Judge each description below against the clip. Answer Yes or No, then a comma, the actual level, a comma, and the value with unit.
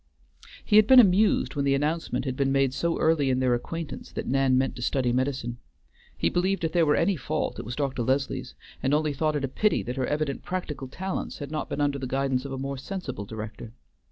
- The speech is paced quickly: Yes, fast, 230 wpm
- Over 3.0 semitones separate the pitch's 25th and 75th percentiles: Yes, average, 3.7 semitones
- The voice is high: No, medium, 140 Hz